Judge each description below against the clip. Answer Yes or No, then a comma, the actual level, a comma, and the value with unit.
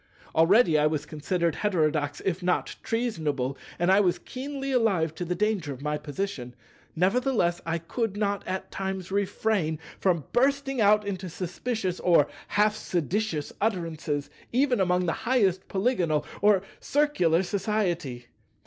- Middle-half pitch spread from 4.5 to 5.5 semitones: Yes, average, 4.8 semitones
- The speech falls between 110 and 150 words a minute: Yes, average, 140 wpm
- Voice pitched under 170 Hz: No, medium, 185 Hz